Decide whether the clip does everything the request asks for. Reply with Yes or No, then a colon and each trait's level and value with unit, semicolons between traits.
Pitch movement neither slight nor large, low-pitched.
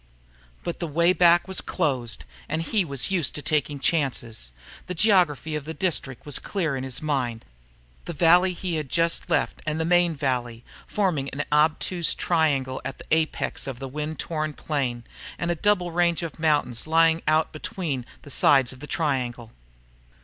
No: average, 3.9 semitones; medium, 155 Hz